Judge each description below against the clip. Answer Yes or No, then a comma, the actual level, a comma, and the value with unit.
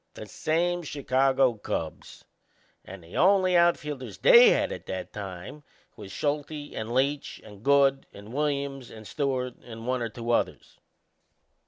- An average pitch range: Yes, average, 4.8 semitones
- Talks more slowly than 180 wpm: Yes, average, 145 wpm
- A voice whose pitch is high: No, low, 135 Hz